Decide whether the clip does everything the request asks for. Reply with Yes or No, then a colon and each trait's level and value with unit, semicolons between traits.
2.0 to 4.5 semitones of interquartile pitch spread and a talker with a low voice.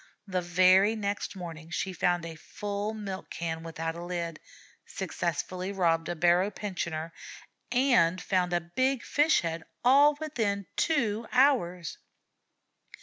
No: average, 3.9 semitones; medium, 185 Hz